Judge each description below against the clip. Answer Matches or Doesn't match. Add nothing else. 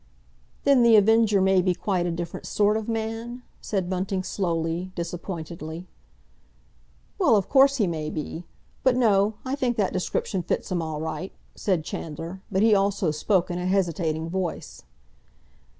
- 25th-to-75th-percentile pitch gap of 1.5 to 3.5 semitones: Doesn't match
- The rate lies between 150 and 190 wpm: Matches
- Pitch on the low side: Doesn't match